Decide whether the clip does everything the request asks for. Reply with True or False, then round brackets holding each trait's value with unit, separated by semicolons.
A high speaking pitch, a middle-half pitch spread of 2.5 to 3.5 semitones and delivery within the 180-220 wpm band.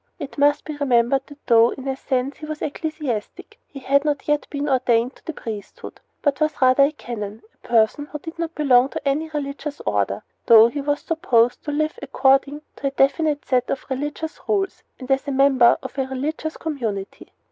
True (275 Hz; 3.1 semitones; 200 wpm)